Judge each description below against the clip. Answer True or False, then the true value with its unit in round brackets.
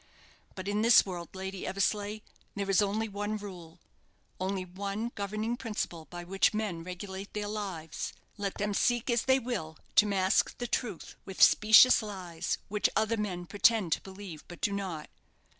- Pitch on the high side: True (200 Hz)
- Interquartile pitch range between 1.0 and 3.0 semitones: True (2.5 semitones)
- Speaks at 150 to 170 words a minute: True (165 wpm)